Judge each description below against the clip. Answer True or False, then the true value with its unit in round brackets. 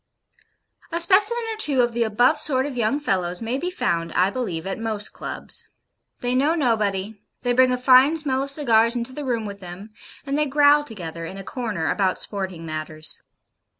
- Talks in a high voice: True (235 Hz)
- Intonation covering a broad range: True (6.2 semitones)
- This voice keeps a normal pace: True (190 wpm)